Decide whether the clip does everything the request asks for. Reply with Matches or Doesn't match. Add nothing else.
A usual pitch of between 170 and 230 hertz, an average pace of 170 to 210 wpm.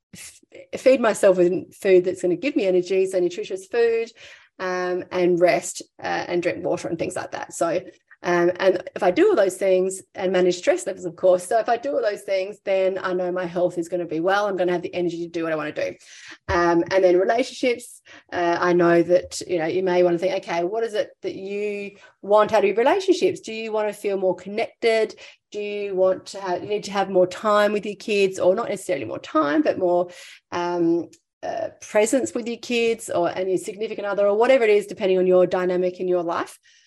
Doesn't match